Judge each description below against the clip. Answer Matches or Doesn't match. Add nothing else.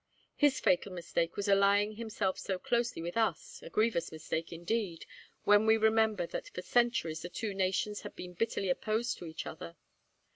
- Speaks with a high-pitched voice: Matches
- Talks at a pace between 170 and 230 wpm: Matches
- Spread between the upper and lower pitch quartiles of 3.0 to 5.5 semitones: Matches